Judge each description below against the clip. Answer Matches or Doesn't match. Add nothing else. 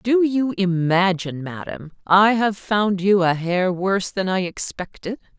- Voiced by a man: Doesn't match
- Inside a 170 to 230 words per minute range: Doesn't match